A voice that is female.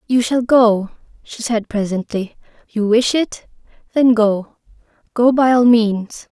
Yes: female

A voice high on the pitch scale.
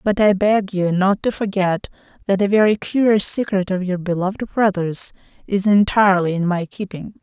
Yes: high, 195 Hz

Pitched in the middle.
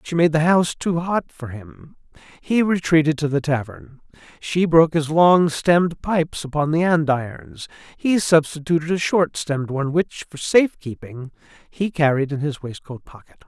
Yes: medium, 155 Hz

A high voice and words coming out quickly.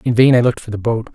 No: low, 115 Hz; fast, 365 wpm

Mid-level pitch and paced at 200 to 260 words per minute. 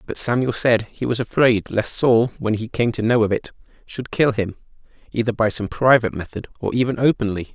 No: low, 115 Hz; fast, 205 wpm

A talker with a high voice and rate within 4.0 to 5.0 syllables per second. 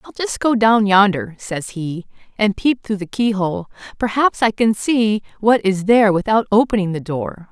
Yes: high, 210 Hz; 4.6 syllables/s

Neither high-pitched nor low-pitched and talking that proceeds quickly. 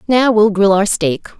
No: high, 205 Hz; fast, 215 wpm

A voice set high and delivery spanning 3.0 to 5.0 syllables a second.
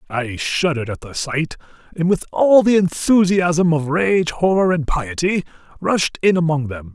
No: medium, 165 Hz; 4.4 syllables/s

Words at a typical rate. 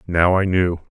Yes: average, 190 wpm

